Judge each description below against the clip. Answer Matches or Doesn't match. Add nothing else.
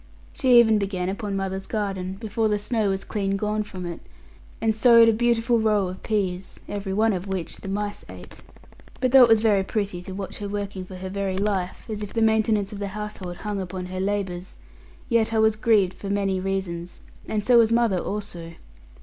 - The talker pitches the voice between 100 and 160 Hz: Doesn't match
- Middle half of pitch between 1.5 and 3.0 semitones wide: Matches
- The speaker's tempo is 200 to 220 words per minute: Matches